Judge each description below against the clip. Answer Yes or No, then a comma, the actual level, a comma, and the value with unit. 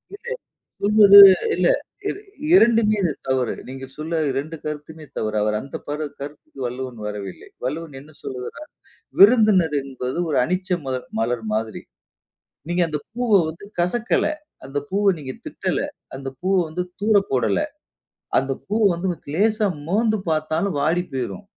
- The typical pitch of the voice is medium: Yes, medium, 155 Hz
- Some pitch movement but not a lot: No, wide, 7.0 semitones